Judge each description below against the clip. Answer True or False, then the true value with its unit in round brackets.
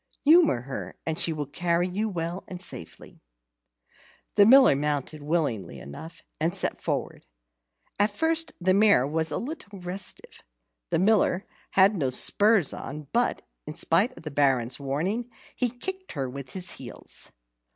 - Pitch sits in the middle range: True (175 Hz)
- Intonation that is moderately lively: False (6.3 semitones)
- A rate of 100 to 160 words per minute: True (150 wpm)